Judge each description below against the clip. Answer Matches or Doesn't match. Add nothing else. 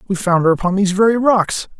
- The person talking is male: Matches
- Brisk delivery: Matches